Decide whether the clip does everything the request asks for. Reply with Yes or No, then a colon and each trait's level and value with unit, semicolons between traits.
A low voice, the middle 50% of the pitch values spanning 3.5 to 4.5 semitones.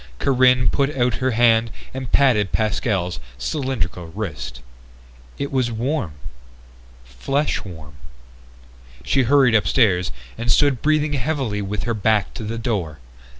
No: low, 115 Hz; wide, 5.4 semitones